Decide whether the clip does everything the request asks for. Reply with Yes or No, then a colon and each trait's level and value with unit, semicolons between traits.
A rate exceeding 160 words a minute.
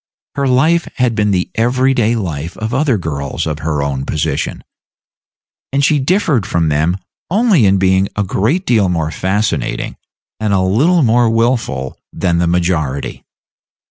No: average, 155 wpm